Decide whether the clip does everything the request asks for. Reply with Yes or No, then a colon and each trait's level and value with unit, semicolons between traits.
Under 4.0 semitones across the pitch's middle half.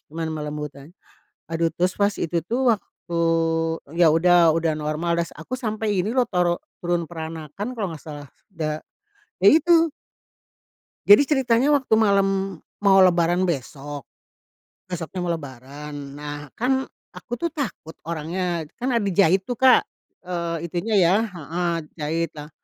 No: average, 4.3 semitones